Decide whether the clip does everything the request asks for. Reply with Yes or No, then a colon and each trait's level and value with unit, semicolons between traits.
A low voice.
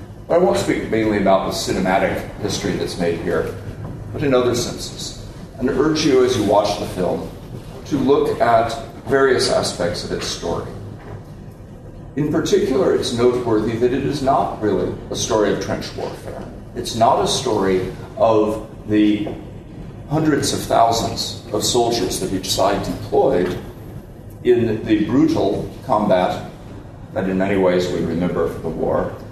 Yes: low, 115 Hz